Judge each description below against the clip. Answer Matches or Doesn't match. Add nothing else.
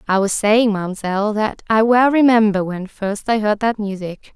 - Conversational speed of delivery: Matches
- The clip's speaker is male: Doesn't match